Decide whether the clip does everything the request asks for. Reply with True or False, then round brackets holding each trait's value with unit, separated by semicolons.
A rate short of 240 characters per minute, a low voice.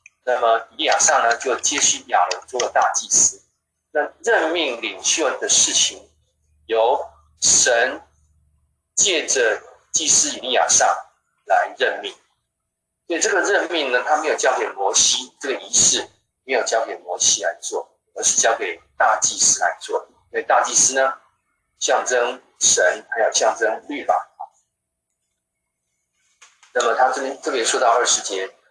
True (210 characters per minute; 75 Hz)